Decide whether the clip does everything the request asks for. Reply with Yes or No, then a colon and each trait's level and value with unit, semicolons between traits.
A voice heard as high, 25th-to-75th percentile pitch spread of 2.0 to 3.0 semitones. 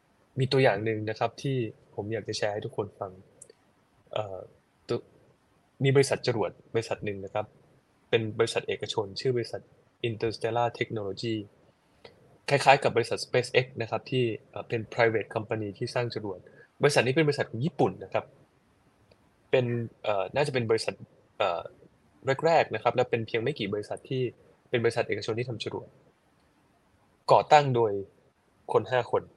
No: low, 115 Hz; average, 2.7 semitones